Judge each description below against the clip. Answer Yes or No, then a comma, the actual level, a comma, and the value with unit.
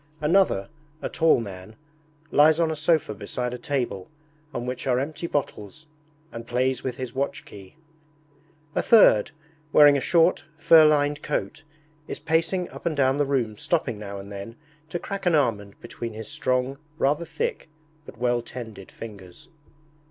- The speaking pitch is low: Yes, low, 130 Hz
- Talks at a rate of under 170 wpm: Yes, average, 160 wpm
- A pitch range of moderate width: No, wide, 5.7 semitones